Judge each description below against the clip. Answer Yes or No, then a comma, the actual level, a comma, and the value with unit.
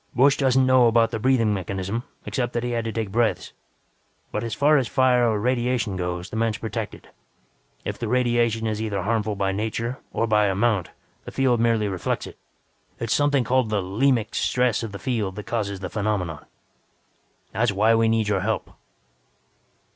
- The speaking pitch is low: Yes, low, 115 Hz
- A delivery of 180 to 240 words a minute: Yes, average, 185 wpm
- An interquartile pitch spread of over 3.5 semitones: No, average, 2.8 semitones